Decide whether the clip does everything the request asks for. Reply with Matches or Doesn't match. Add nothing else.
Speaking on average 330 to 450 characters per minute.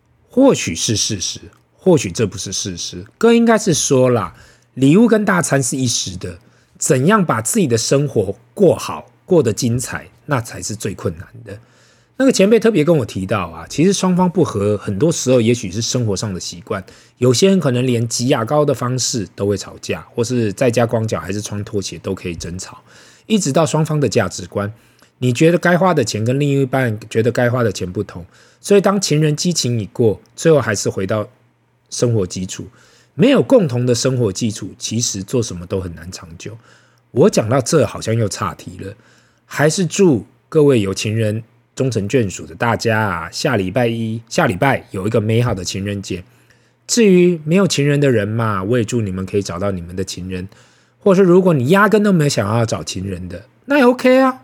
Doesn't match